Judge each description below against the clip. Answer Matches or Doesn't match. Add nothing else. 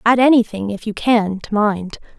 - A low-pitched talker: Doesn't match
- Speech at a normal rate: Matches